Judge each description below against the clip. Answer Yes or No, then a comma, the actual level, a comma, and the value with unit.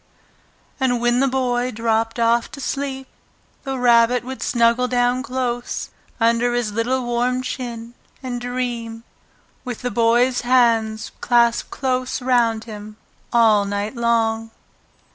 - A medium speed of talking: No, slow, 125 wpm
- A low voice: No, high, 240 Hz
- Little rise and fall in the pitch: Yes, narrow, 1.6 semitones